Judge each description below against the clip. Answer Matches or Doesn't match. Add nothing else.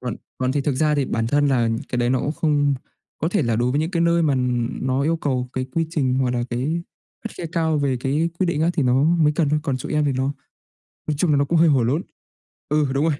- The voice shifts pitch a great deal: Doesn't match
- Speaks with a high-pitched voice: Doesn't match